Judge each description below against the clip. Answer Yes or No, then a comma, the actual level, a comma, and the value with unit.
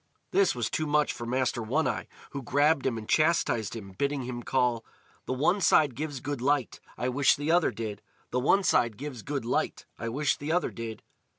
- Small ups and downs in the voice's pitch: No, average, 4.0 semitones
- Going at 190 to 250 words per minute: Yes, fast, 205 wpm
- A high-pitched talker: No, low, 130 Hz